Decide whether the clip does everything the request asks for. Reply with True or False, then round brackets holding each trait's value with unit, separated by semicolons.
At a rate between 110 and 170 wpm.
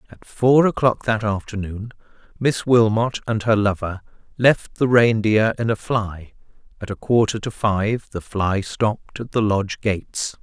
True (160 wpm)